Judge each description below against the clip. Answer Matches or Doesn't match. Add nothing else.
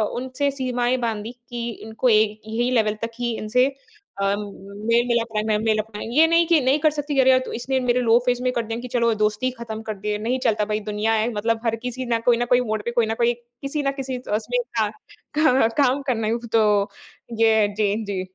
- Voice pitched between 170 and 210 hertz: Doesn't match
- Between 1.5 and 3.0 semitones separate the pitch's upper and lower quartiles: Matches